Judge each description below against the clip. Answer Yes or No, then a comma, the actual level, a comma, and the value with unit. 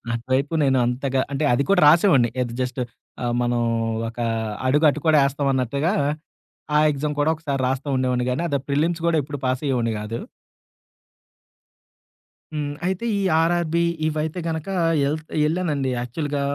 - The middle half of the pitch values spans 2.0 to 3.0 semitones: No, average, 3.5 semitones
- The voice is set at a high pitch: No, medium, 140 Hz